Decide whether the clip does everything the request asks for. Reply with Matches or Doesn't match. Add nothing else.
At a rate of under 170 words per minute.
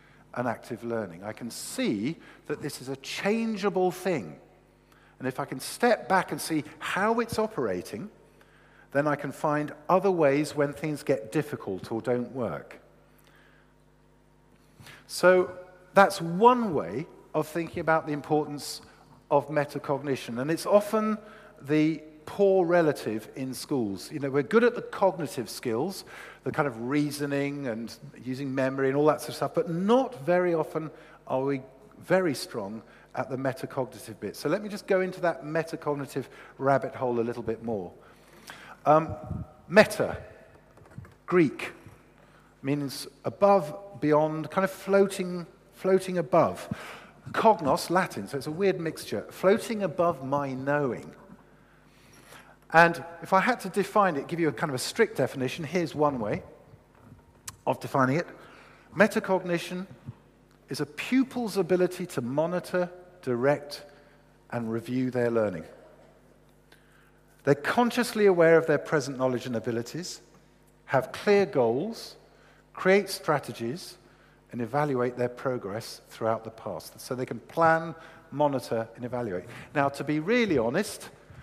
Matches